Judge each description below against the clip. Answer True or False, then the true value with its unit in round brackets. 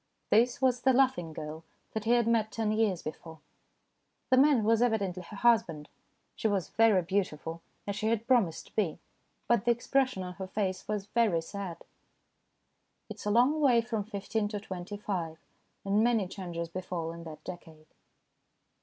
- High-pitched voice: True (205 Hz)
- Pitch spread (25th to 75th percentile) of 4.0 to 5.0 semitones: True (4.6 semitones)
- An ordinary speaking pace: True (170 wpm)